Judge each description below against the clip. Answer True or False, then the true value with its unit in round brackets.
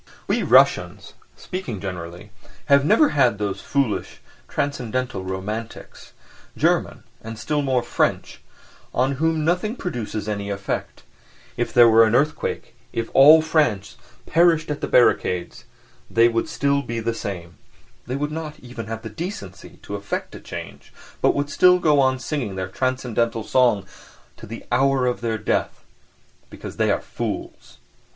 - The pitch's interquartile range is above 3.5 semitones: True (5.1 semitones)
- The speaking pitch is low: True (120 Hz)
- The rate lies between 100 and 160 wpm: True (145 wpm)